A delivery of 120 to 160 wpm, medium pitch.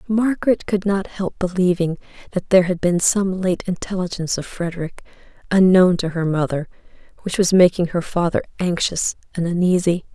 Yes: average, 155 wpm; medium, 180 Hz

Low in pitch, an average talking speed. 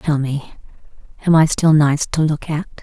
No: medium, 150 Hz; average, 190 wpm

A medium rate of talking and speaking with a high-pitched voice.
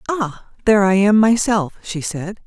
Yes: average, 170 wpm; high, 200 Hz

